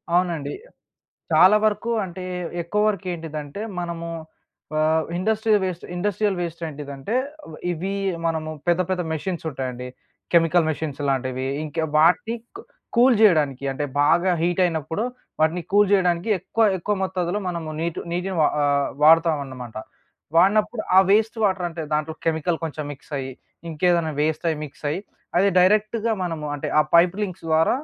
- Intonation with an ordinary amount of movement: Yes, average, 3.5 semitones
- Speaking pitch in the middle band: Yes, medium, 170 Hz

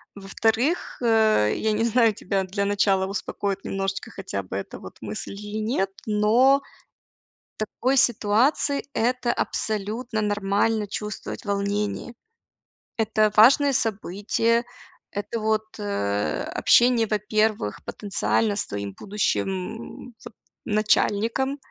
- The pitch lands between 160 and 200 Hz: No, high, 210 Hz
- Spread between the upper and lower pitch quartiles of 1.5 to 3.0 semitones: Yes, narrow, 2.4 semitones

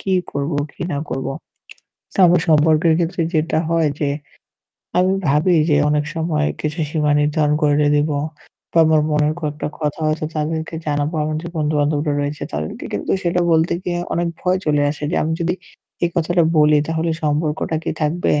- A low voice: No, medium, 155 Hz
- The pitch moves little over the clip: Yes, narrow, 1.8 semitones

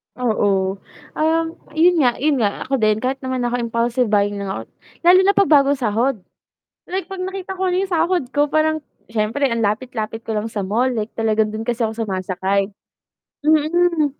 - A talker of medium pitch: No, high, 245 Hz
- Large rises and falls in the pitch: Yes, wide, 6.5 semitones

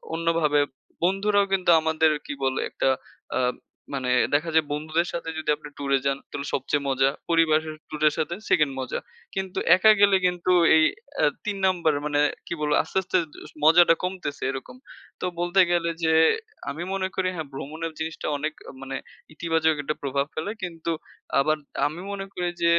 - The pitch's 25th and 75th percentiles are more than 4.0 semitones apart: No, average, 3.0 semitones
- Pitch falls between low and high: Yes, medium, 160 Hz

